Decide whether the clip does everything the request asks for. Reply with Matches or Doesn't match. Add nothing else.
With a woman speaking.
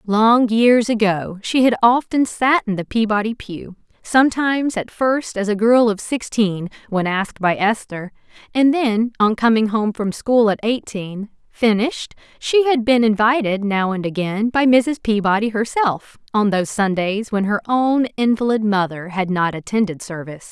Matches